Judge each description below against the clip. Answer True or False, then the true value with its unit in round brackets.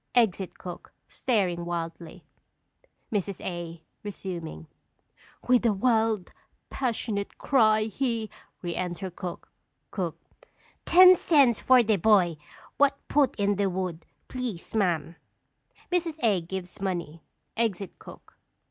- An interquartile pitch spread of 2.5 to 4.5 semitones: False (5.0 semitones)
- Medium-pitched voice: False (200 Hz)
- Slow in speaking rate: True (115 wpm)